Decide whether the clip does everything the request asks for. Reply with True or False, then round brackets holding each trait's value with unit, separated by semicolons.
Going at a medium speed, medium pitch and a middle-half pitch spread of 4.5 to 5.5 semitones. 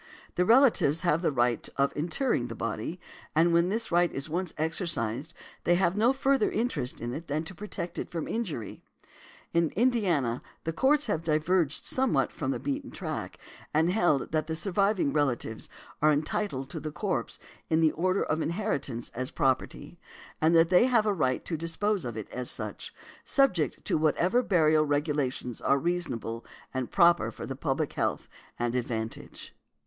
True (170 wpm; 160 Hz; 5.2 semitones)